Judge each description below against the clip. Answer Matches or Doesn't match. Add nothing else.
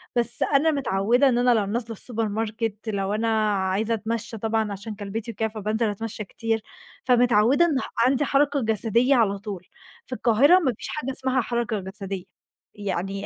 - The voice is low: Doesn't match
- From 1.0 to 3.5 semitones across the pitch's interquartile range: Matches